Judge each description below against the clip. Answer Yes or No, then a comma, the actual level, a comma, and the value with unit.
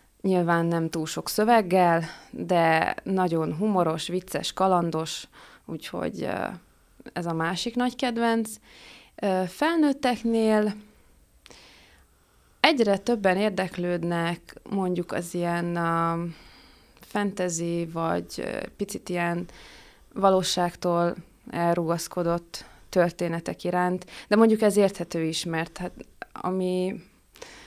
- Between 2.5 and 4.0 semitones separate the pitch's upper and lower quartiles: Yes, average, 3.2 semitones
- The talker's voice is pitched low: No, medium, 180 Hz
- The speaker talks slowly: Yes, slow, 85 wpm